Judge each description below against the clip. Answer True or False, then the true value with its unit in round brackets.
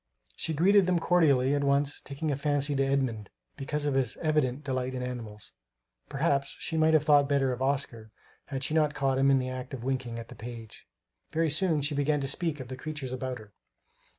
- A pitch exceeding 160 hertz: False (140 Hz)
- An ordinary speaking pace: False (210 wpm)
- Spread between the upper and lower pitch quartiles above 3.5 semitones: False (2.6 semitones)